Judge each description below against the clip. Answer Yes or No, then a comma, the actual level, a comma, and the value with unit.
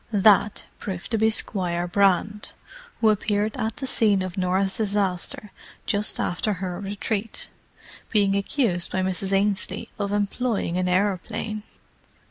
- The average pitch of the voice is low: No, high, 200 Hz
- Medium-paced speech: No, slow, 130 wpm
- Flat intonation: Yes, narrow, 2.2 semitones